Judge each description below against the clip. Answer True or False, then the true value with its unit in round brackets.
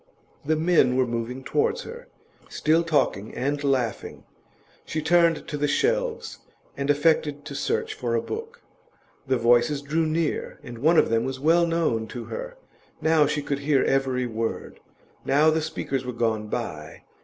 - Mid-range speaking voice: True (145 Hz)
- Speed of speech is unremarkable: True (165 wpm)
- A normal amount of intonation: True (4.7 semitones)